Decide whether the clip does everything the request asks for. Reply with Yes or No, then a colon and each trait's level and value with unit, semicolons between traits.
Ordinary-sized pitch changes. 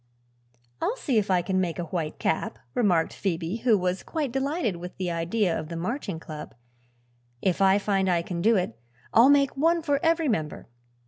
No: wide, 7.1 semitones